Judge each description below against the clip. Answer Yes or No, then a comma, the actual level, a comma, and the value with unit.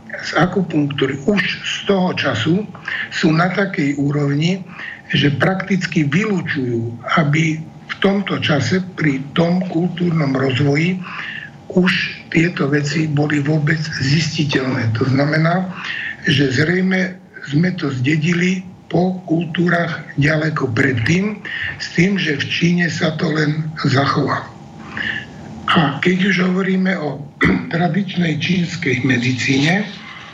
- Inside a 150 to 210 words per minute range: No, slow, 110 wpm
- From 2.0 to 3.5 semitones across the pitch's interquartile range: No, average, 4.0 semitones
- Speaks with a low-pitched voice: No, medium, 165 Hz